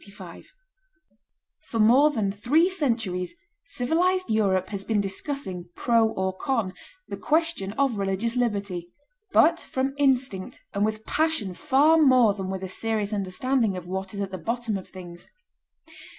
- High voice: Yes, high, 220 Hz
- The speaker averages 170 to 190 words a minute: No, average, 150 wpm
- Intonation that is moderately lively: No, wide, 6.2 semitones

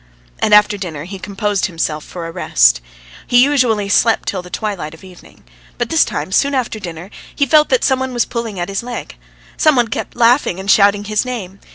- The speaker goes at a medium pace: No, fast, 210 wpm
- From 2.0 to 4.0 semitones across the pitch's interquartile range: No, average, 5.0 semitones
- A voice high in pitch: Yes, high, 205 Hz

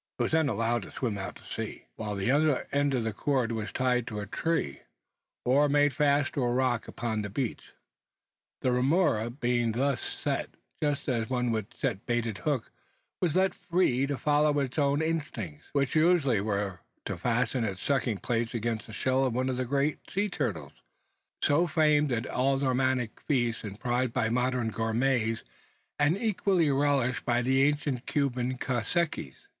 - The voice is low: Yes, low, 130 Hz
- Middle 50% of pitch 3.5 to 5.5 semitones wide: Yes, average, 4.0 semitones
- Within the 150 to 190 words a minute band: Yes, average, 180 wpm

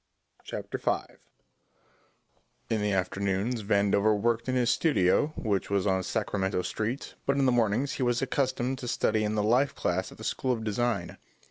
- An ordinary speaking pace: Yes, average, 170 wpm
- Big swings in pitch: No, average, 3.7 semitones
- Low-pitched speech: Yes, low, 110 Hz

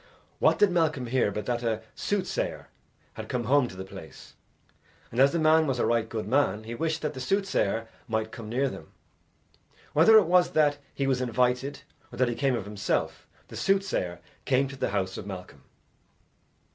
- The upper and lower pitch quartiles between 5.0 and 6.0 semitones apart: Yes, wide, 5.5 semitones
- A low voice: Yes, low, 125 Hz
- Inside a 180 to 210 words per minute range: Yes, average, 190 wpm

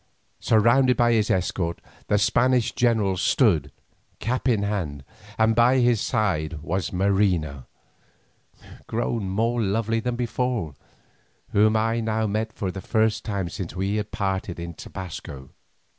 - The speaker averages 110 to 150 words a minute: Yes, slow, 135 wpm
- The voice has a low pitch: Yes, low, 105 Hz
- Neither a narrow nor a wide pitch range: Yes, average, 3.6 semitones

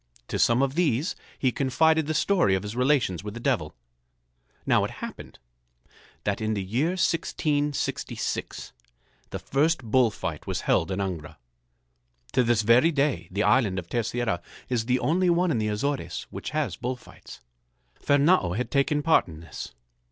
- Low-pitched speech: Yes, low, 125 Hz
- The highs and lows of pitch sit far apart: Yes, wide, 6.1 semitones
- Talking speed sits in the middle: Yes, average, 165 wpm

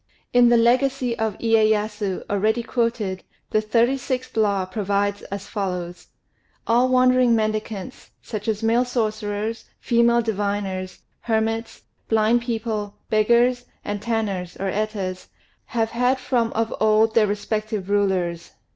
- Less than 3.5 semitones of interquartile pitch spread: Yes, narrow, 2.6 semitones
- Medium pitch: No, high, 220 Hz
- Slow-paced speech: Yes, slow, 120 wpm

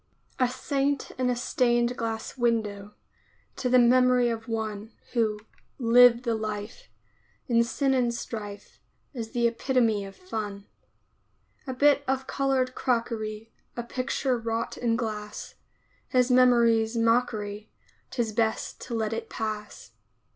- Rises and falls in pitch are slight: Yes, narrow, 2.3 semitones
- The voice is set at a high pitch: Yes, high, 235 Hz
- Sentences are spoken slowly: Yes, slow, 130 wpm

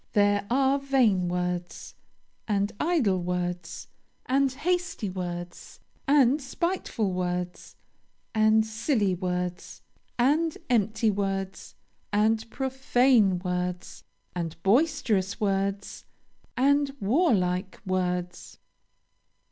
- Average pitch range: No, wide, 6.5 semitones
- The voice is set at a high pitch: Yes, high, 205 Hz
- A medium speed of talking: No, slow, 85 wpm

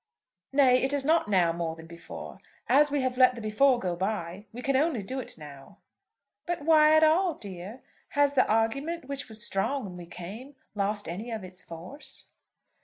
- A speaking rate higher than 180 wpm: Yes, average, 190 wpm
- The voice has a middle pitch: No, high, 235 Hz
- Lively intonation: Yes, wide, 7.1 semitones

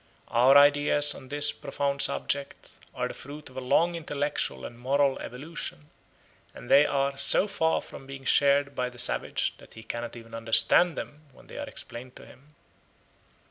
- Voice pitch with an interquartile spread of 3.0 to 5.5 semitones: No, narrow, 2.4 semitones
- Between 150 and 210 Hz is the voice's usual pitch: No, medium, 140 Hz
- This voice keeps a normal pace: Yes, average, 175 wpm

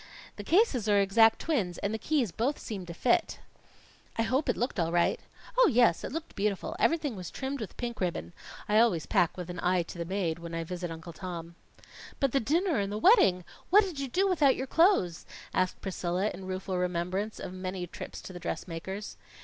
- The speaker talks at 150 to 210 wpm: Yes, fast, 205 wpm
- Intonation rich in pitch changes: Yes, wide, 6.4 semitones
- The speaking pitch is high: Yes, high, 195 Hz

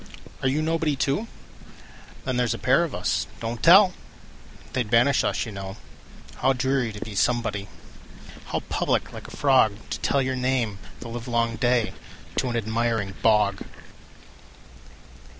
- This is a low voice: Yes, low, 120 Hz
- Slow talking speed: Yes, slow, 130 wpm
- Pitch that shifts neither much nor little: Yes, average, 3.2 semitones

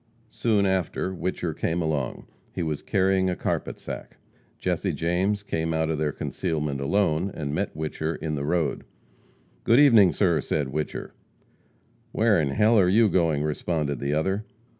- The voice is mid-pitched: No, very low, 85 Hz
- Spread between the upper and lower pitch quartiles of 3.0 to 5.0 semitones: Yes, average, 4.0 semitones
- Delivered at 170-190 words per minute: No, average, 160 wpm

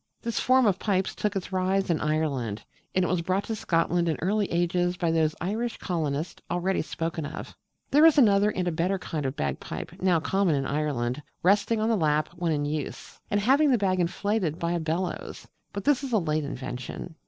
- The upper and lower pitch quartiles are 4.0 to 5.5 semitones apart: Yes, average, 4.4 semitones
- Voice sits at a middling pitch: Yes, medium, 175 Hz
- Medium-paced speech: No, fast, 210 wpm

